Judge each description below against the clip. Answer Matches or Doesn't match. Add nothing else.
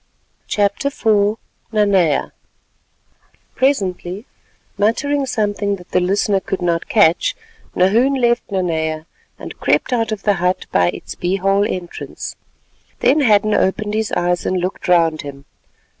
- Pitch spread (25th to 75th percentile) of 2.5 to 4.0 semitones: Matches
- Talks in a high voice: Matches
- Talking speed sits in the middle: Doesn't match